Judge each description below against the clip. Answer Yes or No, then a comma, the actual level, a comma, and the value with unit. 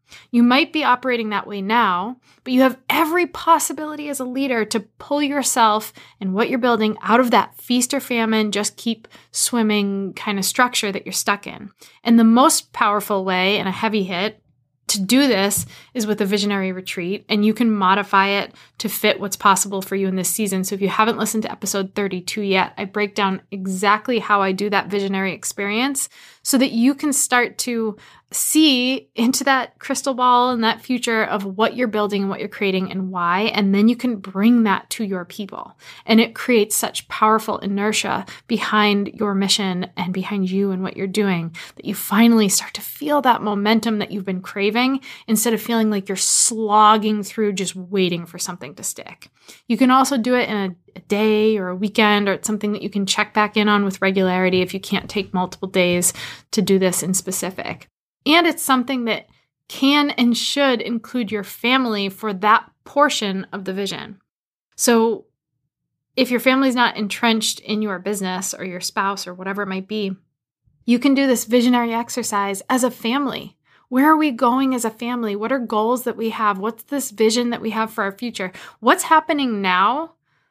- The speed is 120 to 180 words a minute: No, average, 195 wpm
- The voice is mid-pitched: No, high, 215 Hz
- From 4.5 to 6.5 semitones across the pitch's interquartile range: No, average, 3.7 semitones